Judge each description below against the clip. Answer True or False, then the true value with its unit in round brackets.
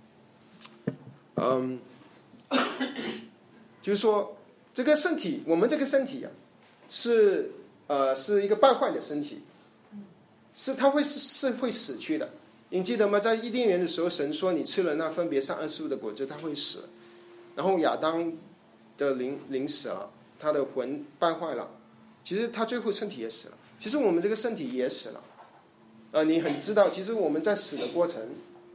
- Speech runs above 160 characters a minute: True (240 characters per minute)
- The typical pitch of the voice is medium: True (175 Hz)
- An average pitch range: False (9.0 semitones)